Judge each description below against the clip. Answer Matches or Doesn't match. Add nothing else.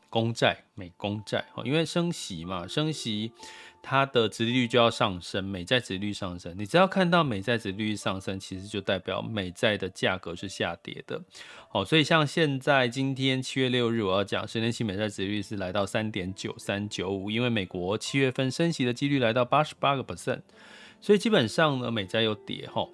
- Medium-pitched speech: Doesn't match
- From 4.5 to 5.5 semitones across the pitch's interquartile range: Matches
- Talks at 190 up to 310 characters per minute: Doesn't match